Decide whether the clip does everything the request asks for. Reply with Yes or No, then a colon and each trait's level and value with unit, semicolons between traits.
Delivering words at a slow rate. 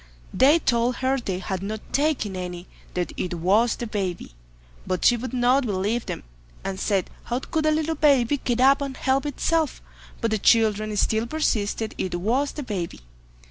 No: average, 170 wpm